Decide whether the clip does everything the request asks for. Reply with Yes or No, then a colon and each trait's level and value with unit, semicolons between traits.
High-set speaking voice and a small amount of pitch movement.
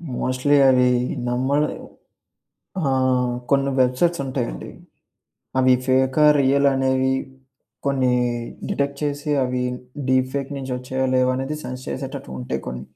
No: low, 130 Hz; narrow, 1.6 semitones